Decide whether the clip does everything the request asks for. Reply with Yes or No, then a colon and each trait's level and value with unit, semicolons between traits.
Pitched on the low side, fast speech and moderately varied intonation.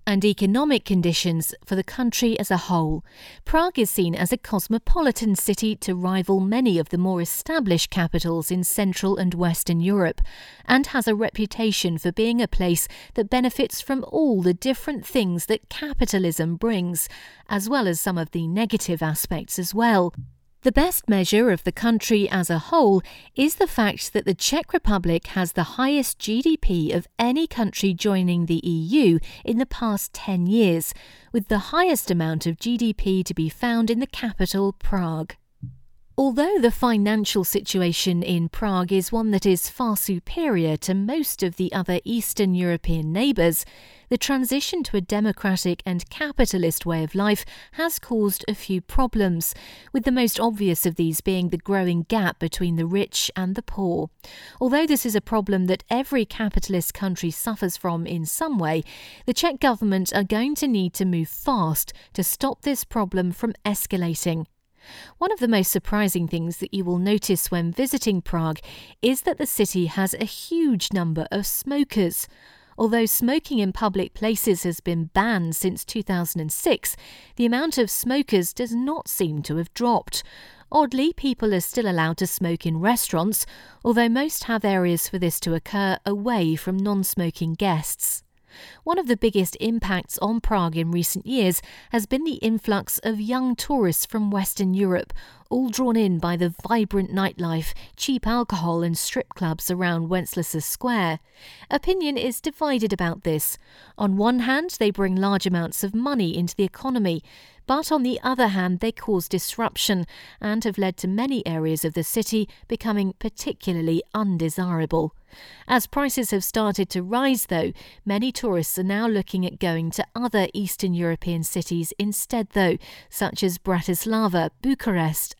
No: high, 200 Hz; fast, 165 wpm; average, 4.9 semitones